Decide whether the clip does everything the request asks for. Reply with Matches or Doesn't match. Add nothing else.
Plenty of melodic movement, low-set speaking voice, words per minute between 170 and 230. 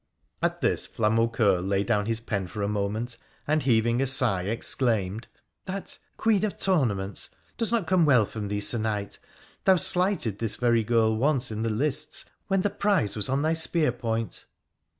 Matches